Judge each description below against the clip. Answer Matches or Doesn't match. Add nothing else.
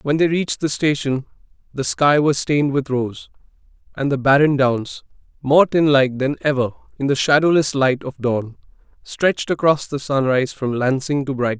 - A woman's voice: Doesn't match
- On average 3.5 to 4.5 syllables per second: Doesn't match